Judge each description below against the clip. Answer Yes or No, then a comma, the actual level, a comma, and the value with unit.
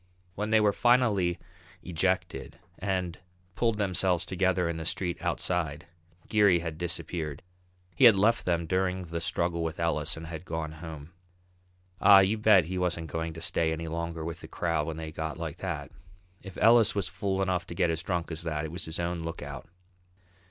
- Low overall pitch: Yes, very low, 85 Hz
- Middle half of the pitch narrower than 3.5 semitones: Yes, average, 2.7 semitones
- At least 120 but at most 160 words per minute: No, average, 185 wpm